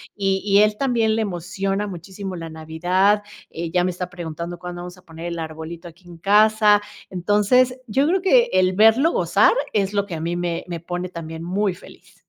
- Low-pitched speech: No, medium, 185 Hz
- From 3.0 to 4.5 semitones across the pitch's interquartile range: Yes, average, 3.3 semitones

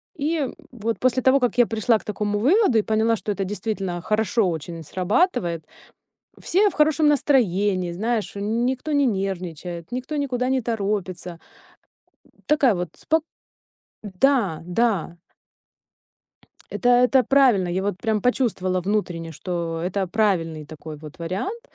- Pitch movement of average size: No, wide, 5.8 semitones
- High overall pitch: Yes, high, 210 Hz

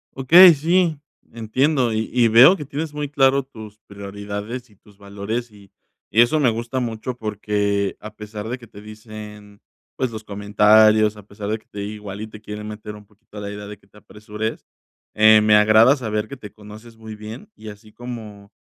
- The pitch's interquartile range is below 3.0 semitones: Yes, narrow, 2.4 semitones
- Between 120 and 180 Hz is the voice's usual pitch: No, low, 110 Hz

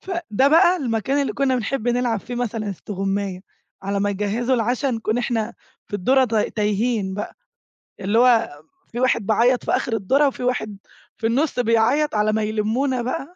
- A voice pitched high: Yes, high, 230 Hz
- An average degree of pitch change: Yes, average, 3.4 semitones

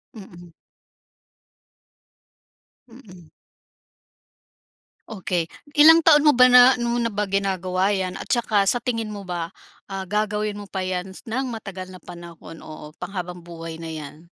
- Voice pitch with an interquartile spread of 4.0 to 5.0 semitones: Yes, average, 4.4 semitones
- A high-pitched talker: Yes, high, 195 Hz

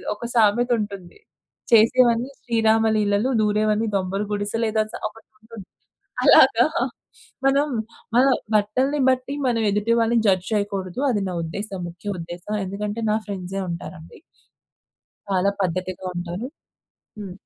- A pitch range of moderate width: Yes, average, 3.1 semitones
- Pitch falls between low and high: No, high, 210 Hz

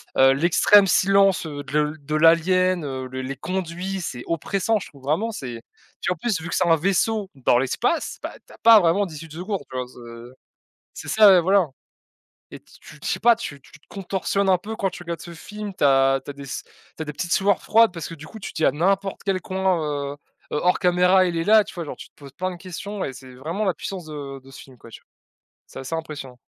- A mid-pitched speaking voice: Yes, medium, 170 Hz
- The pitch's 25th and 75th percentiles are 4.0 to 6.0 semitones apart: Yes, average, 5.1 semitones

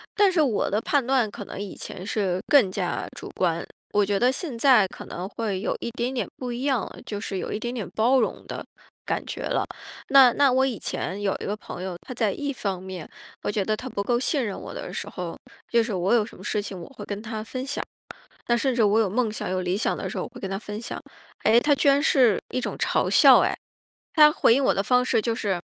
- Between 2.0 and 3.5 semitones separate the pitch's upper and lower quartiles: No, average, 4.2 semitones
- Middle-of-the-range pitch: No, high, 225 Hz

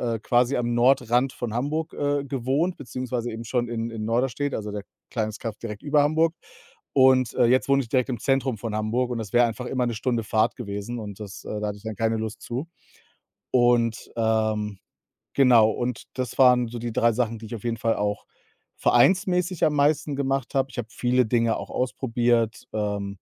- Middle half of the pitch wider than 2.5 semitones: Yes, average, 2.9 semitones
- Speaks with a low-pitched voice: Yes, low, 120 Hz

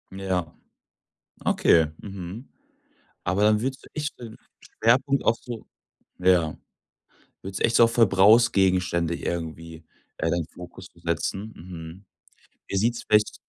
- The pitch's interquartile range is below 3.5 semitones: No, average, 4.7 semitones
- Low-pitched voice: Yes, very low, 95 Hz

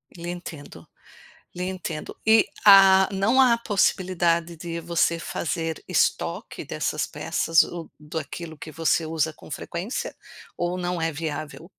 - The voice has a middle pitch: Yes, medium, 170 Hz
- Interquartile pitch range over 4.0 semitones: No, narrow, 2.5 semitones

